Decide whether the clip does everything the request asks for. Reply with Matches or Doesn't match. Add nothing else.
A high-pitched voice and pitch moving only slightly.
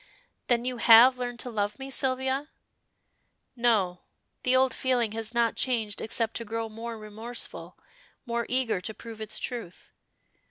Matches